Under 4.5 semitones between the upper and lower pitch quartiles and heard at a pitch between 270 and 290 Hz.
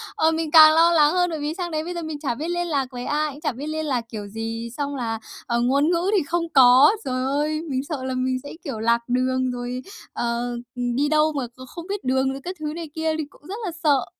Yes: average, 3.9 semitones; very high, 285 Hz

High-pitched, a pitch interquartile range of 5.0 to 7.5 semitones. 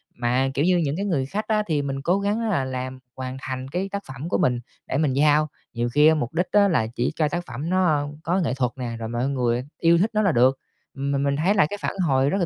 No: medium, 145 Hz; average, 5.3 semitones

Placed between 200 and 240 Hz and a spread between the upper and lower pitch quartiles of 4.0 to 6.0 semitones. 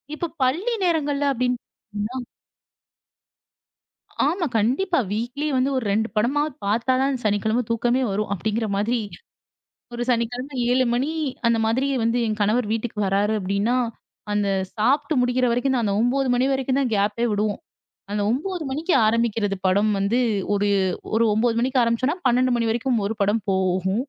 No: high, 235 Hz; average, 3.5 semitones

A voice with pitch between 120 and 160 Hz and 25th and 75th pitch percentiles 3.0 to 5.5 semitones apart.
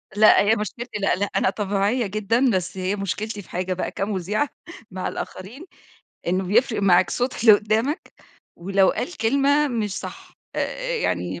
No: high, 205 Hz; average, 3.7 semitones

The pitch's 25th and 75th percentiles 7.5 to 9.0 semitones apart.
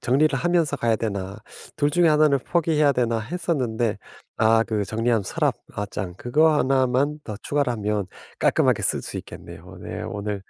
No: wide, 5.6 semitones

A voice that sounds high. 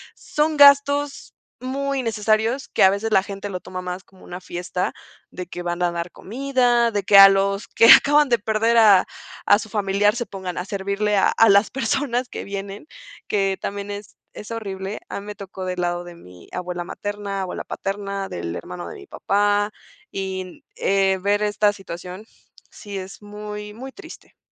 Yes: high, 200 Hz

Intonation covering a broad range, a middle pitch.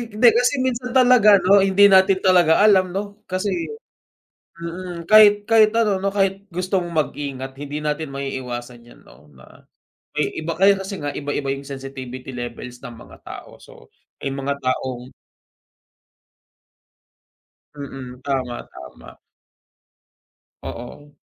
Yes: wide, 6.8 semitones; medium, 160 Hz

